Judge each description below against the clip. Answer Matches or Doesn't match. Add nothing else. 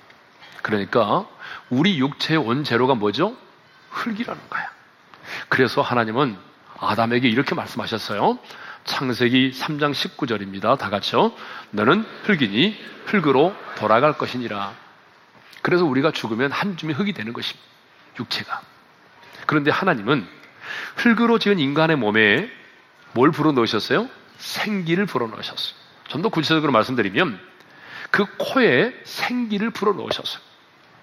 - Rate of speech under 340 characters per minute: Matches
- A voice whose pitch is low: Doesn't match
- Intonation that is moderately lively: Doesn't match